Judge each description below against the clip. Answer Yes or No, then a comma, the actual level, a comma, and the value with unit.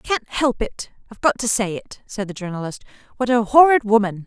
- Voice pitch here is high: Yes, high, 225 Hz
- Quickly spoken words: No, average, 195 wpm